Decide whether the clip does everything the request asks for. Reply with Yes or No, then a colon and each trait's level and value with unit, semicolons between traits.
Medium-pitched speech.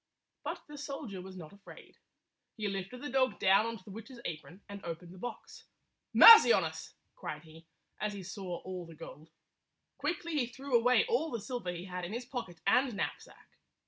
No: high, 205 Hz